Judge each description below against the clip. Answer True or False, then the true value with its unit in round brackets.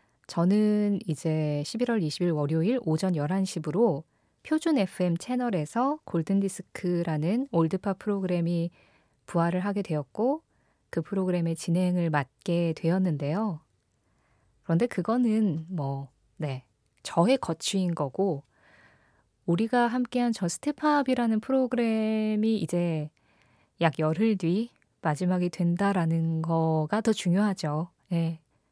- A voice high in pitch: False (175 Hz)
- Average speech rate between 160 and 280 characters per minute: True (245 characters per minute)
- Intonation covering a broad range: False (5.0 semitones)